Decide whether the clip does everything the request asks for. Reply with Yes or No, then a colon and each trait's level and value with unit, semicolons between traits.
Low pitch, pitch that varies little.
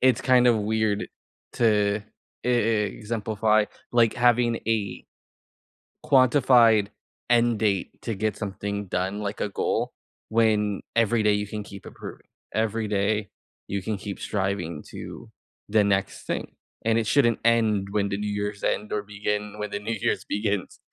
Yes: low, 105 Hz; narrow, 1.9 semitones